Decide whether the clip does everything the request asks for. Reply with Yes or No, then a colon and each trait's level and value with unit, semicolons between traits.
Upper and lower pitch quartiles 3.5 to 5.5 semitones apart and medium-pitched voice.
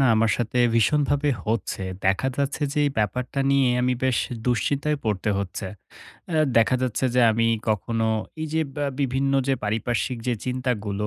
No: average, 3.9 semitones; low, 125 Hz